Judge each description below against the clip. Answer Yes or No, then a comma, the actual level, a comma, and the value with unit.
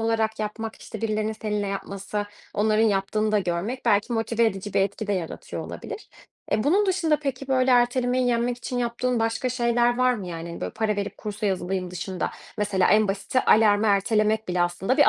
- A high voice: Yes, high, 215 Hz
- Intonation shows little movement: No, average, 3.3 semitones